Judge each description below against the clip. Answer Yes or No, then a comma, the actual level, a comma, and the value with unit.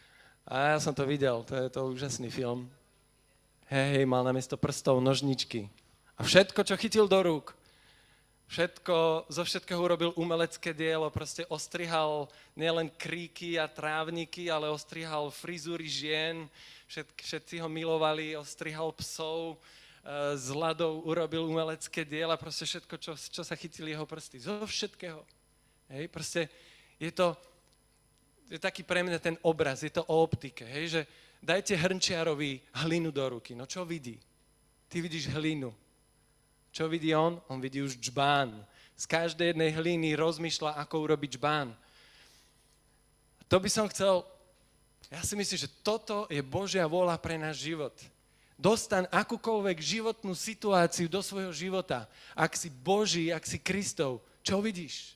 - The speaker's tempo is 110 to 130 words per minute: No, average, 145 wpm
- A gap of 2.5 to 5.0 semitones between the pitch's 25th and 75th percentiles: Yes, average, 2.9 semitones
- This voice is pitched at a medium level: Yes, medium, 160 Hz